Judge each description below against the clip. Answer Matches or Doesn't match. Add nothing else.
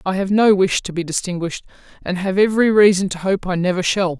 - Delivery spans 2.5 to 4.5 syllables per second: Doesn't match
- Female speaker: Matches